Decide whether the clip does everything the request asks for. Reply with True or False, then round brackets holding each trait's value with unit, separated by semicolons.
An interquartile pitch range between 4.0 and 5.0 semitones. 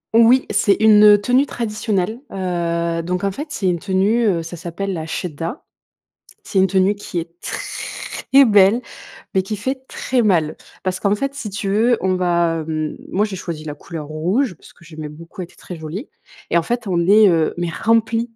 True (4.4 semitones)